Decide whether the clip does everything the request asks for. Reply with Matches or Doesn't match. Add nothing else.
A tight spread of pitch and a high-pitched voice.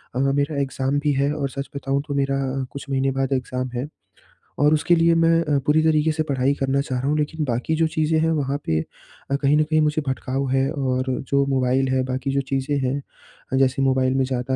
Doesn't match